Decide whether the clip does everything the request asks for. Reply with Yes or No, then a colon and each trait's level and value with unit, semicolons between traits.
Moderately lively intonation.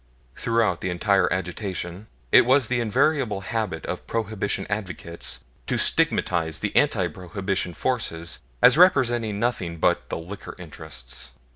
Yes: average, 5.0 semitones